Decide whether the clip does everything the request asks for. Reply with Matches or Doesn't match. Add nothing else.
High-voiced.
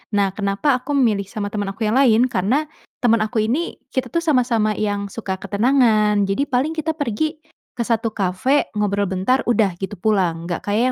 Matches